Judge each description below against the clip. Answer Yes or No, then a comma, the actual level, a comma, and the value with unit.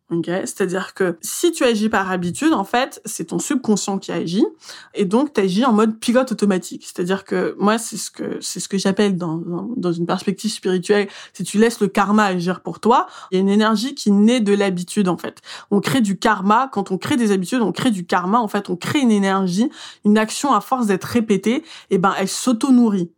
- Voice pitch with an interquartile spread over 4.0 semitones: No, average, 3.7 semitones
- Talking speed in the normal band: No, fast, 230 wpm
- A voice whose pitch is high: Yes, high, 205 Hz